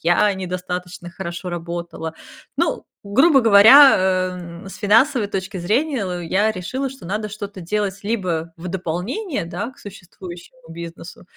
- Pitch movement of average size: Yes, average, 3.7 semitones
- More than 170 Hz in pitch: Yes, high, 190 Hz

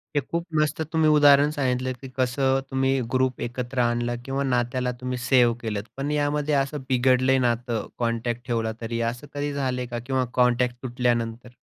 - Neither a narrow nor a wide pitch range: No, narrow, 2.2 semitones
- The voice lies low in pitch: Yes, low, 125 Hz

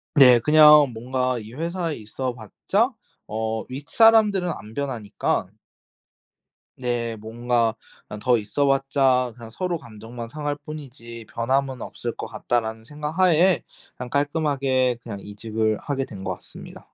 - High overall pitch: No, low, 125 Hz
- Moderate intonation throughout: Yes, average, 4.5 semitones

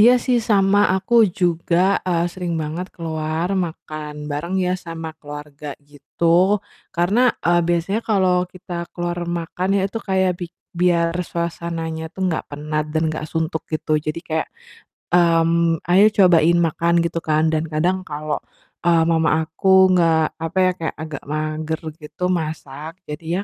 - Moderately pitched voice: Yes, medium, 170 Hz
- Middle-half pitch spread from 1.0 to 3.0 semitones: Yes, narrow, 2.5 semitones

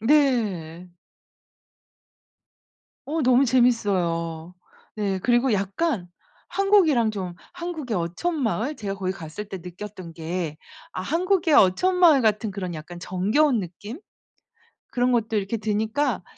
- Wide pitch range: Yes, wide, 6.8 semitones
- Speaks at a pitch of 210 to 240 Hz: Yes, high, 215 Hz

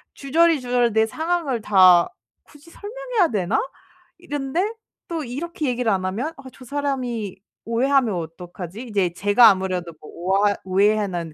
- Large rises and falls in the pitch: Yes, wide, 7.2 semitones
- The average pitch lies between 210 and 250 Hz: Yes, high, 235 Hz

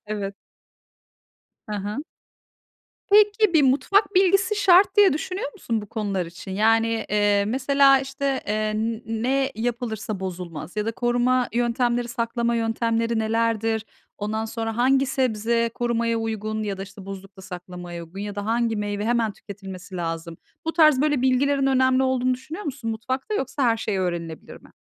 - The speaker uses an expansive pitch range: No, average, 4.1 semitones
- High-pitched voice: Yes, high, 230 Hz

